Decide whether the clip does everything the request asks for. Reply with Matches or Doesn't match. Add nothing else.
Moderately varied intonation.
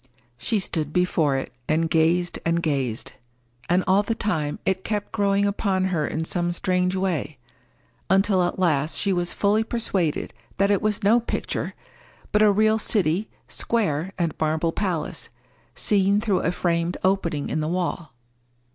Matches